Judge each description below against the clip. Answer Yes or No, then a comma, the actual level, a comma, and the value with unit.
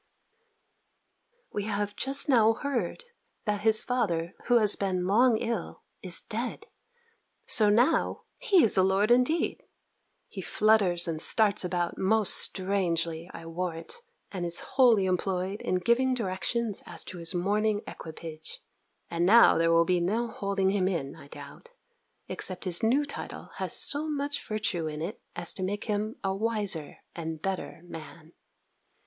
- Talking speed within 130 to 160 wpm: Yes, average, 150 wpm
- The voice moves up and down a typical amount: Yes, average, 4.5 semitones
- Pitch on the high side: Yes, high, 195 Hz